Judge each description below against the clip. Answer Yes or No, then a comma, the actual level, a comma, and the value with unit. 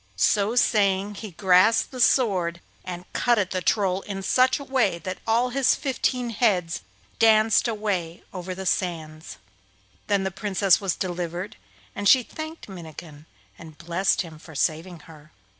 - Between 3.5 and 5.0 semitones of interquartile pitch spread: Yes, average, 4.2 semitones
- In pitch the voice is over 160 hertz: Yes, high, 190 Hz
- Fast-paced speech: No, average, 155 wpm